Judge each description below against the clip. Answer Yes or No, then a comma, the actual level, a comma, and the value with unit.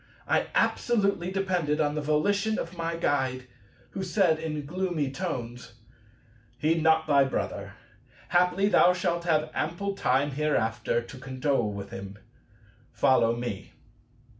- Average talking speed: No, slow, 130 wpm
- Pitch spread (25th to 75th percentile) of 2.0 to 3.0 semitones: No, wide, 5.4 semitones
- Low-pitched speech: No, medium, 155 Hz